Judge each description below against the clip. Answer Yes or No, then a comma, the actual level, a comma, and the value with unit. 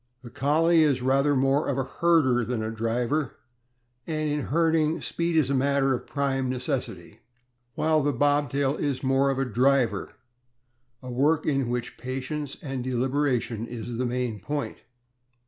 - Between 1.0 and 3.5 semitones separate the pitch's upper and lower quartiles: Yes, average, 2.8 semitones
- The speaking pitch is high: No, low, 135 Hz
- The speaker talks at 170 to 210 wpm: No, average, 160 wpm